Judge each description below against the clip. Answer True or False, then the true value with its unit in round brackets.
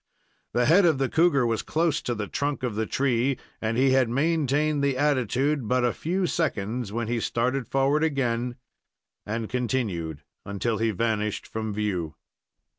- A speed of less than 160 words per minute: False (165 wpm)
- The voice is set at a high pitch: False (125 Hz)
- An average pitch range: True (4.0 semitones)